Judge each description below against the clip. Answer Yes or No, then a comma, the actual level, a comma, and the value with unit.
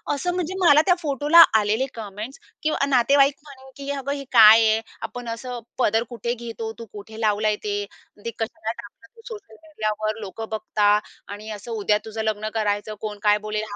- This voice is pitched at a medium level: No, high, 225 Hz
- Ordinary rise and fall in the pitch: Yes, average, 4.0 semitones